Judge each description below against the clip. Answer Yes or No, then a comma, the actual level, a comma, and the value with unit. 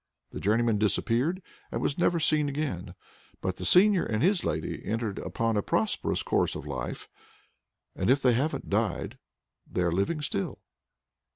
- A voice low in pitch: Yes, low, 115 Hz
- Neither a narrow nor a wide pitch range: No, wide, 7.6 semitones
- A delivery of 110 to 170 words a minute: Yes, average, 155 wpm